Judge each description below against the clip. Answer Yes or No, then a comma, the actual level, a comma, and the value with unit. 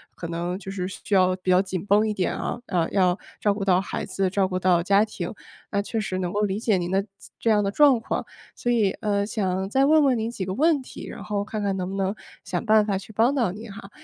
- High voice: Yes, high, 200 Hz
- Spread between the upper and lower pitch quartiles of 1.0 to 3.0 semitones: Yes, average, 2.7 semitones